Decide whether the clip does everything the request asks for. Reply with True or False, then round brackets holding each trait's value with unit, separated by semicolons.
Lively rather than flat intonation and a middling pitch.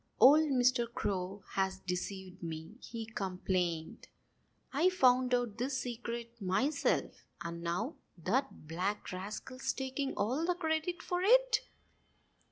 False (6.3 semitones; 235 Hz)